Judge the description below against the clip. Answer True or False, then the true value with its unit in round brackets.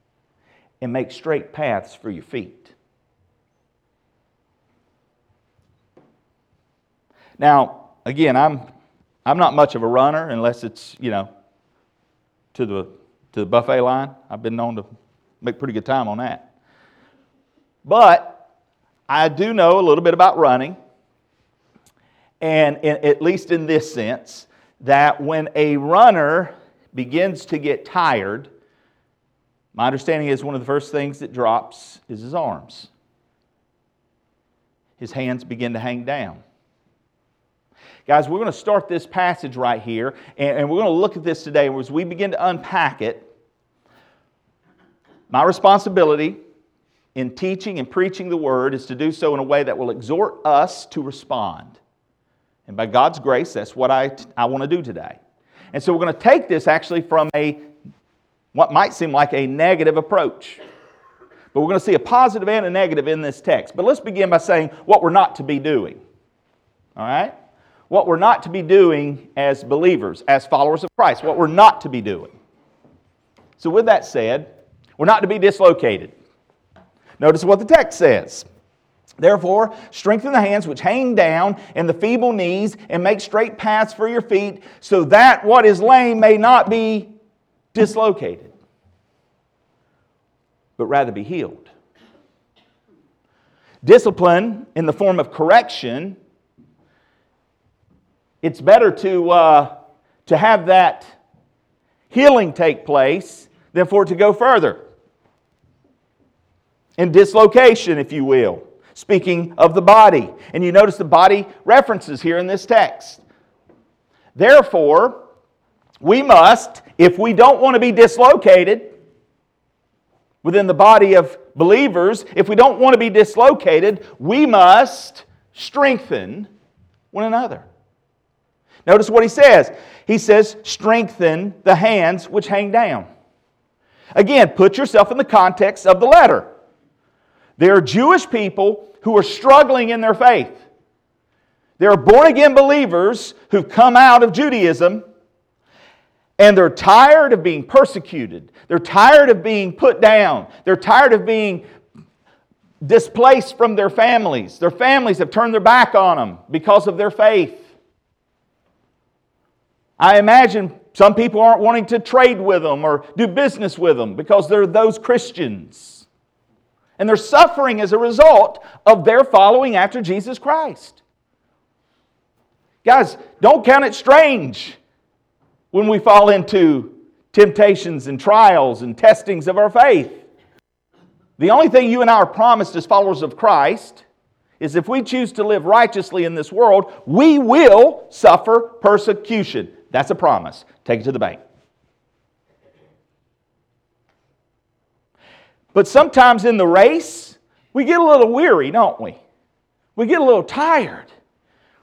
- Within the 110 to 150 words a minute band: True (145 wpm)